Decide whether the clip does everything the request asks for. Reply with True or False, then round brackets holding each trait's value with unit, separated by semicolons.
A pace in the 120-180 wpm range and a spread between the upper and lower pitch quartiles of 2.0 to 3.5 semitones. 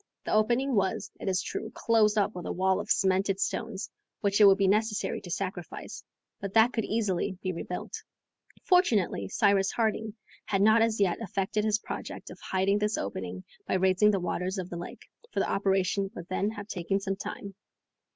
False (190 wpm; 2.4 semitones)